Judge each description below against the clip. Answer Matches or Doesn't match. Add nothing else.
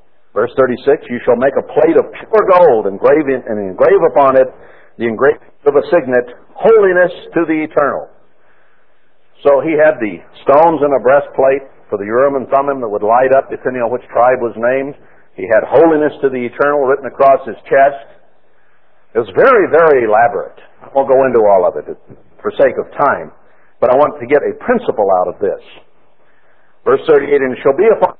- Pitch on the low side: Doesn't match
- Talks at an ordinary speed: Matches